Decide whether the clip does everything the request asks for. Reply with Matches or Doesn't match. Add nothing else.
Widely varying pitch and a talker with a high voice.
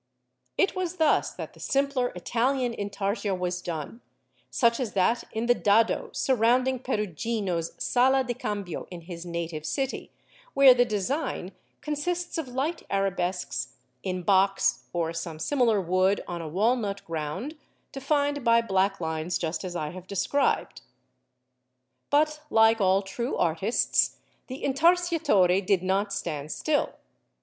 Matches